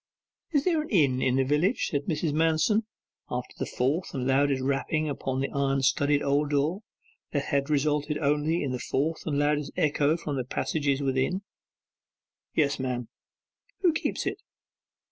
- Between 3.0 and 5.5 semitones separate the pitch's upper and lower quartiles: No, narrow, 2.5 semitones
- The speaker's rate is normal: Yes, average, 160 wpm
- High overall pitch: No, medium, 145 Hz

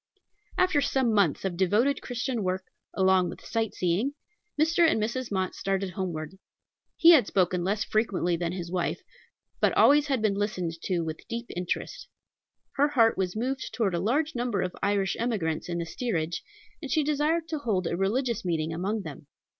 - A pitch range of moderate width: No, wide, 5.8 semitones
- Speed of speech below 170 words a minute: No, average, 180 wpm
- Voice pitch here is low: No, high, 200 Hz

